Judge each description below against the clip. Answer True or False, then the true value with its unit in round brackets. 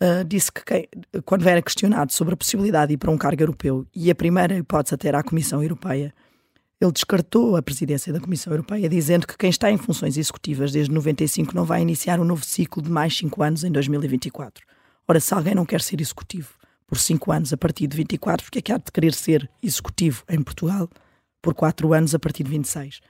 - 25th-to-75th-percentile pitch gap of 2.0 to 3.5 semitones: True (2.8 semitones)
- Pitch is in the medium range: True (160 Hz)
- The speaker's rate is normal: False (220 wpm)